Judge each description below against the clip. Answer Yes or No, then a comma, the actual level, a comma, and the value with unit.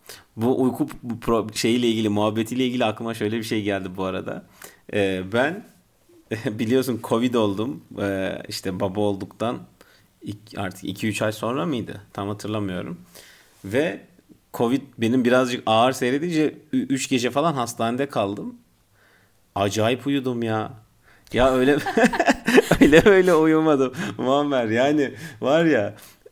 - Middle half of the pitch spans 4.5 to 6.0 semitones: No, average, 4.1 semitones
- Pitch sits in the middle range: No, low, 115 Hz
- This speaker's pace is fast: No, average, 120 wpm